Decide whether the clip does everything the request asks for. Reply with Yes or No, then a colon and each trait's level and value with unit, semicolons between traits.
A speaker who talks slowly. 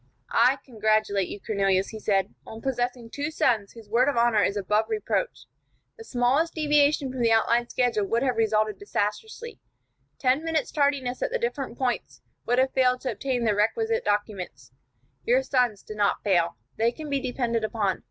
No: average, 175 wpm